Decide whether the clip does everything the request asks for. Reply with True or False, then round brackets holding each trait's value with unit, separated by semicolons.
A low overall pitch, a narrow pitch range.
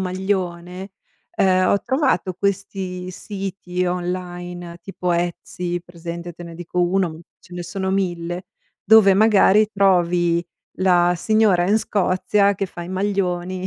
False (180 Hz; 1.9 semitones)